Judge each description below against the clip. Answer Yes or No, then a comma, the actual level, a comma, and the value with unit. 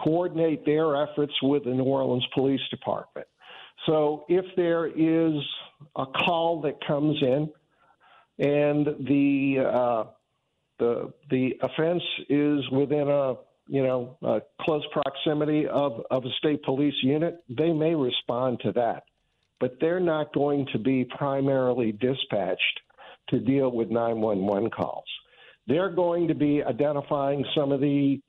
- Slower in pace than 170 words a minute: Yes, slow, 135 wpm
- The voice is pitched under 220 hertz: Yes, medium, 140 Hz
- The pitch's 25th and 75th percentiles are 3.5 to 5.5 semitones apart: No, average, 2.8 semitones